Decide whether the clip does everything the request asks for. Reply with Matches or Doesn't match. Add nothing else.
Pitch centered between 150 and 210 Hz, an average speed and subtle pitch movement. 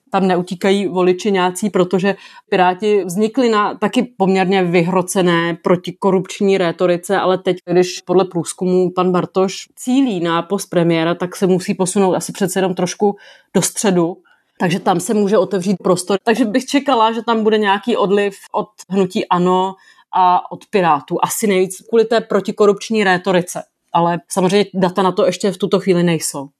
Matches